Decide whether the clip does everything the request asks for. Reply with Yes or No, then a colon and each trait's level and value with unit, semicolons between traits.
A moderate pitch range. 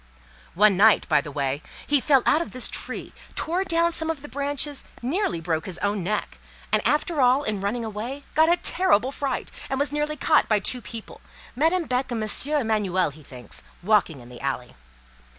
No: wide, 7.2 semitones